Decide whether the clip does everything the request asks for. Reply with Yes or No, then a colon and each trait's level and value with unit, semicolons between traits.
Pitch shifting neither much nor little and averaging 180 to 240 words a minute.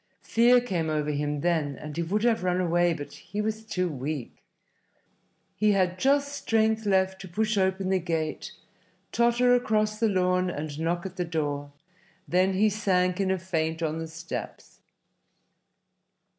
No: average, 4.7 semitones; average, 160 wpm